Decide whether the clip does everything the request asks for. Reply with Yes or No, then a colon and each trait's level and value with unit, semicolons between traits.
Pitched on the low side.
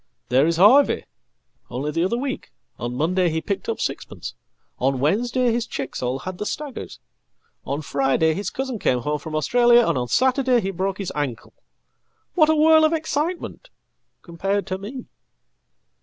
No: high, 195 Hz